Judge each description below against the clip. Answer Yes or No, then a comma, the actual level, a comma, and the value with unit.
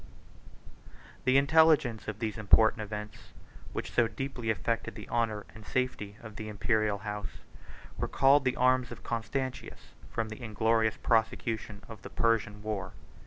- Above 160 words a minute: No, average, 145 wpm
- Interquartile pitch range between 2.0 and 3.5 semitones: Yes, average, 2.7 semitones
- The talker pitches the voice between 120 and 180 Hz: No, low, 110 Hz